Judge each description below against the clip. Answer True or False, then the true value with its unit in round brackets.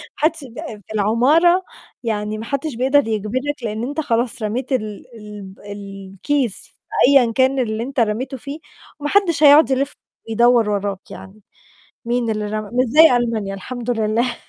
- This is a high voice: True (235 Hz)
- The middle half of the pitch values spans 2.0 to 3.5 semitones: False (4.4 semitones)